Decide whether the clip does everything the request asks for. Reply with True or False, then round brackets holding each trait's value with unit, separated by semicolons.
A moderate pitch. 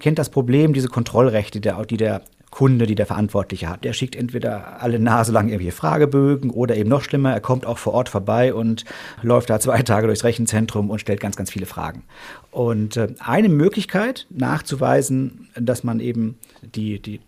False (120 Hz)